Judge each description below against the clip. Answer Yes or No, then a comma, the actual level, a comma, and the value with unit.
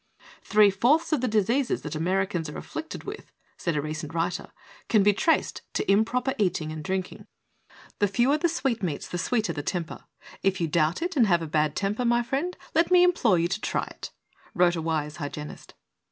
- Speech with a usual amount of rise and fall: No, wide, 6.9 semitones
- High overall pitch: Yes, high, 195 Hz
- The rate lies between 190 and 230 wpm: Yes, average, 195 wpm